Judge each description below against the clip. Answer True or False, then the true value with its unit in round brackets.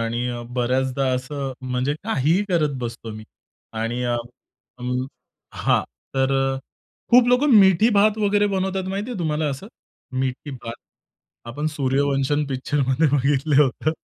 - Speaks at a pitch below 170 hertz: True (140 Hz)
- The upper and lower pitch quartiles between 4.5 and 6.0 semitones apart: True (5.5 semitones)